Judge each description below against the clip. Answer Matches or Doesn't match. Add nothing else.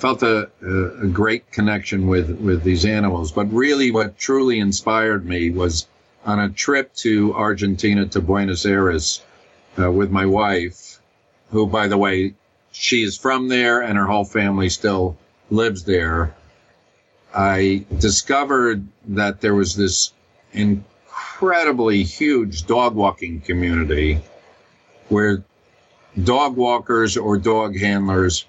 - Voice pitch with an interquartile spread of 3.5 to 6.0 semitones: Doesn't match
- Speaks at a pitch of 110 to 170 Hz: Doesn't match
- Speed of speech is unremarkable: Doesn't match